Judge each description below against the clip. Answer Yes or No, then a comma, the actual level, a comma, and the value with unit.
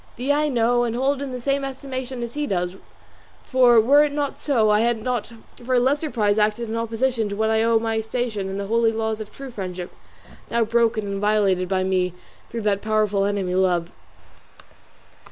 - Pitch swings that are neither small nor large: Yes, average, 3.6 semitones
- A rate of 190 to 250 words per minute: Yes, fast, 205 wpm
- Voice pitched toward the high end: Yes, high, 225 Hz